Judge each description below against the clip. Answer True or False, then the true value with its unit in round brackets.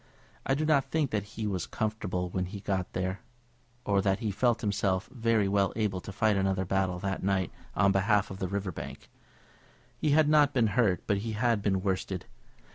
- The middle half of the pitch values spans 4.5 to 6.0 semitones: False (2.9 semitones)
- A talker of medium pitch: False (100 Hz)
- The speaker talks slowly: False (200 wpm)